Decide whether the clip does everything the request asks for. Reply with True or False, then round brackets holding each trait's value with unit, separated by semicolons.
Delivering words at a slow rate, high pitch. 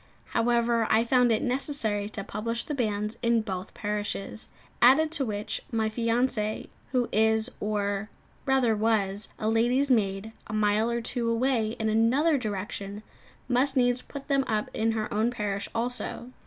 False (155 wpm; 225 Hz)